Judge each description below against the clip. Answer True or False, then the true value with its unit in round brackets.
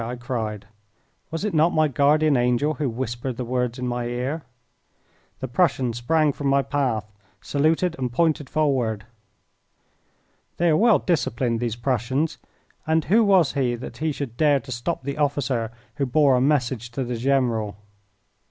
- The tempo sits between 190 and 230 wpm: False (160 wpm)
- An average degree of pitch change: True (4.1 semitones)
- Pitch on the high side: False (135 Hz)